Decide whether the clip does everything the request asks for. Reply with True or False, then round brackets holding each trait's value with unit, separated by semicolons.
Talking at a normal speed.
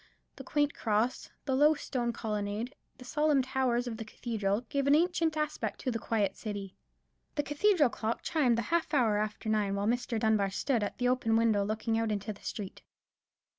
True (190 wpm)